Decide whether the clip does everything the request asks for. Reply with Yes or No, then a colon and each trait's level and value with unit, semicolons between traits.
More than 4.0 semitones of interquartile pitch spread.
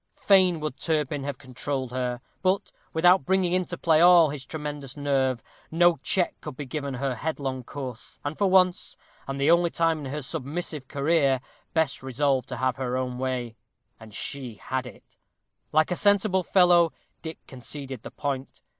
Yes: average, 4.4 semitones